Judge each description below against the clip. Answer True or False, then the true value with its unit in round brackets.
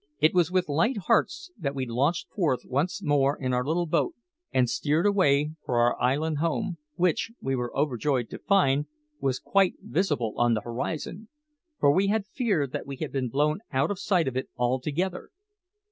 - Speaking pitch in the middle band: True (150 Hz)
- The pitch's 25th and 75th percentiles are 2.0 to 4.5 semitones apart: False (5.6 semitones)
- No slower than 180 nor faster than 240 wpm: True (185 wpm)